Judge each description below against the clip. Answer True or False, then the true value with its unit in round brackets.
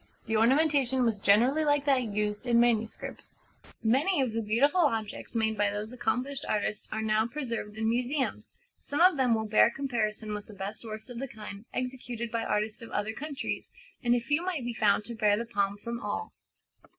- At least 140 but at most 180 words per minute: False (200 wpm)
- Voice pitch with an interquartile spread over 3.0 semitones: True (3.5 semitones)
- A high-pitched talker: True (230 Hz)